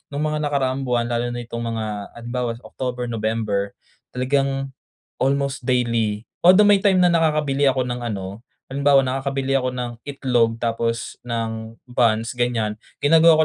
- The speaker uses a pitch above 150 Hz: No, low, 125 Hz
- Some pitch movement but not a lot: Yes, average, 3.2 semitones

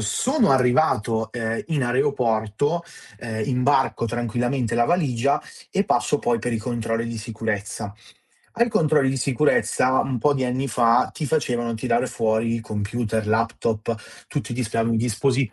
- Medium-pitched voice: No, low, 120 Hz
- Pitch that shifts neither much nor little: Yes, average, 3.0 semitones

